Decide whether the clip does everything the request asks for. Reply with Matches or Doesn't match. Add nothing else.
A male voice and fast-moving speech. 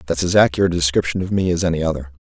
Matches